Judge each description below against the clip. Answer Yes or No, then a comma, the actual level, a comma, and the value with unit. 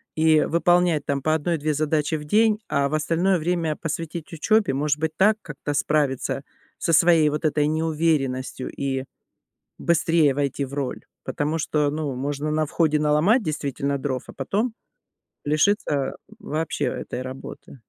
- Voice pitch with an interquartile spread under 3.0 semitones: Yes, narrow, 2.6 semitones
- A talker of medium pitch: Yes, medium, 155 Hz